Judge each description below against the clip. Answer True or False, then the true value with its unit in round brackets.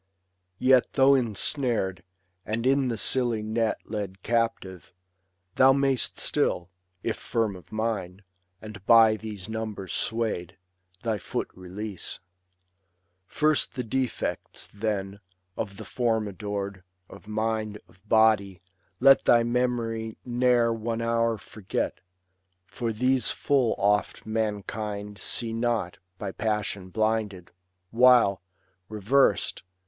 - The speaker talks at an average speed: False (110 wpm)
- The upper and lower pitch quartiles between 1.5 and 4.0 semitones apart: True (2.6 semitones)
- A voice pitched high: False (110 Hz)